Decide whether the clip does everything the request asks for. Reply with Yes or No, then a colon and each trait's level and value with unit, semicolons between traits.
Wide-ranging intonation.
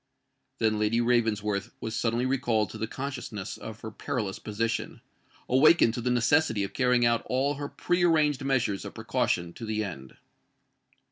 No: average, 3.6 semitones